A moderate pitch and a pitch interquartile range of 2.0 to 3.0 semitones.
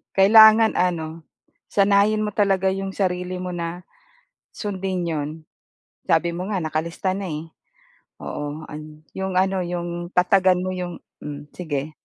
Yes: medium, 180 Hz; average, 2.7 semitones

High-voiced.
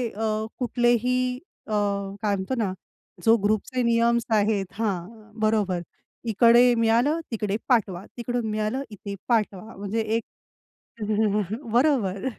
Yes: high, 220 Hz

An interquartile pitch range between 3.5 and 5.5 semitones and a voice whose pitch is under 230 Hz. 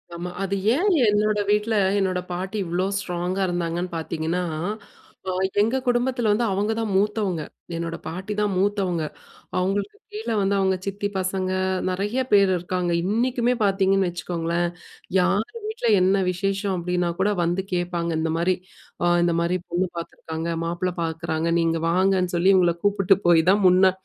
No: average, 2.7 semitones; medium, 185 Hz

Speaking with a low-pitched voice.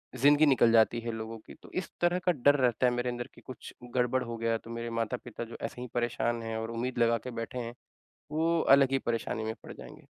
Yes: low, 120 Hz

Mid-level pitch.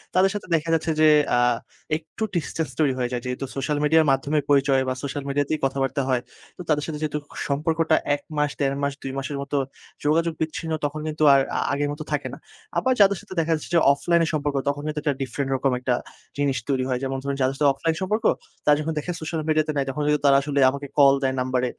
Yes: medium, 145 Hz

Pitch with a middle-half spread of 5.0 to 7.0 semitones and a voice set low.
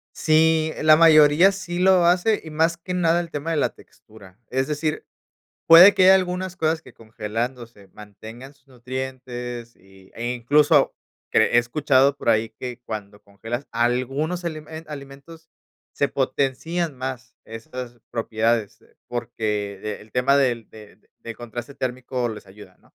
Yes: wide, 5.4 semitones; low, 130 Hz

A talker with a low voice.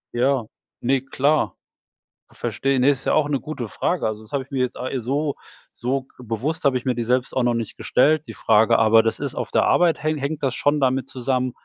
Yes: low, 130 Hz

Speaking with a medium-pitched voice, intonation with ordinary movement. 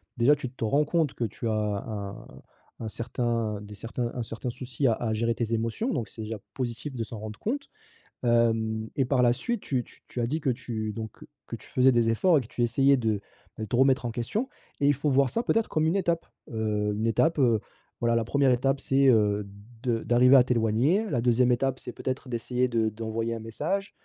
No: low, 120 Hz; average, 3.2 semitones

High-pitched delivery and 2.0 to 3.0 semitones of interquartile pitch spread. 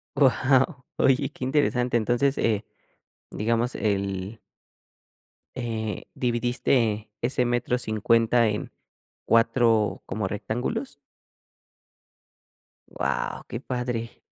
No: low, 120 Hz; narrow, 2.4 semitones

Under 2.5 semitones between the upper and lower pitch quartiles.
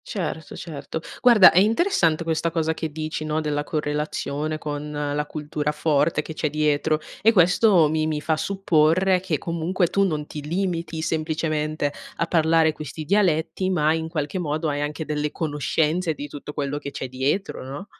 Yes: narrow, 2.1 semitones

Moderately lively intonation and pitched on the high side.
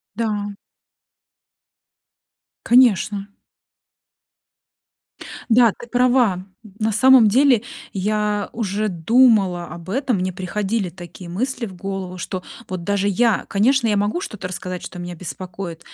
Yes: average, 3.9 semitones; high, 205 Hz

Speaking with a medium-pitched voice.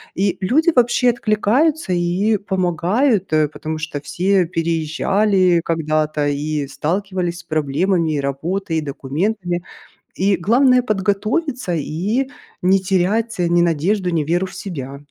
Yes: medium, 180 Hz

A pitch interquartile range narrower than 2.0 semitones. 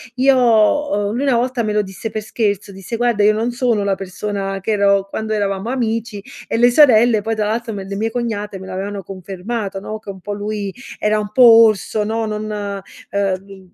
No: narrow, 2.4 semitones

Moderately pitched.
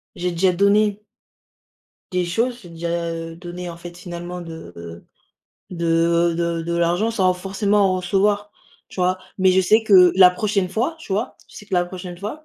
Yes: medium, 180 Hz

